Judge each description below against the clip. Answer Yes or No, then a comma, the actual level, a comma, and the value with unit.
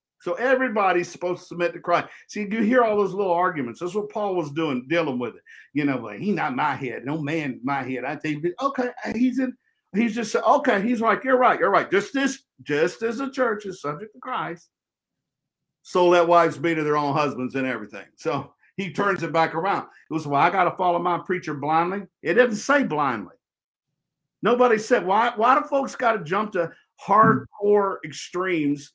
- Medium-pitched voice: Yes, medium, 175 Hz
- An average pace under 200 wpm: No, fast, 205 wpm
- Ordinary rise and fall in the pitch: No, wide, 6.6 semitones